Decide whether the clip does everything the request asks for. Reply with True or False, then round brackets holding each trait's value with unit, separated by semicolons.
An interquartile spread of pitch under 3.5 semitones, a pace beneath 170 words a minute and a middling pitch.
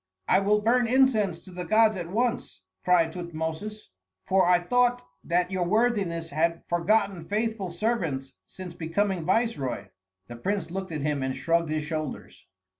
False (4.7 semitones; 155 wpm; 180 Hz)